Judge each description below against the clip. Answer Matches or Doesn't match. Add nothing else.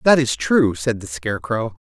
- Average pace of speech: Matches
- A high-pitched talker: Doesn't match